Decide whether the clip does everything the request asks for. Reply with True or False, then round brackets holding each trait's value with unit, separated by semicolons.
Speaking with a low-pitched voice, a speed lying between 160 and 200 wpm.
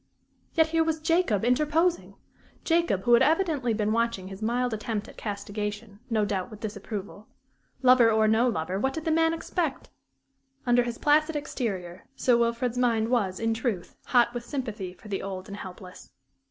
False (230 Hz; 170 wpm)